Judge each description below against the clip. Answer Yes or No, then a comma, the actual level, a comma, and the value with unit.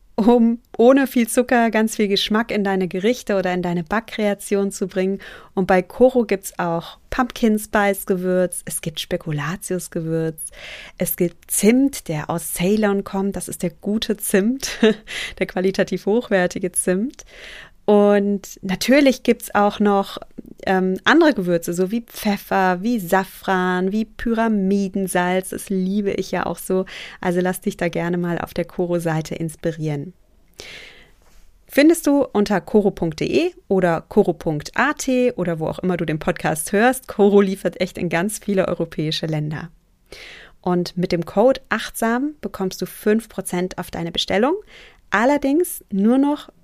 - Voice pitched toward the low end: No, high, 195 Hz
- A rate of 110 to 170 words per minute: Yes, average, 140 wpm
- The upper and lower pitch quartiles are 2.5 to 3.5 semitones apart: No, average, 4.0 semitones